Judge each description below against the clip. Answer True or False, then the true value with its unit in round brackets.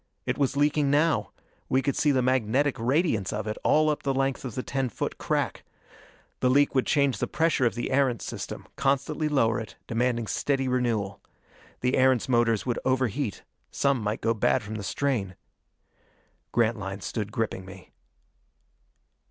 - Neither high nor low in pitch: False (125 Hz)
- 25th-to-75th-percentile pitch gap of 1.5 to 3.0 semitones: False (3.8 semitones)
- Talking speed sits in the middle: True (165 wpm)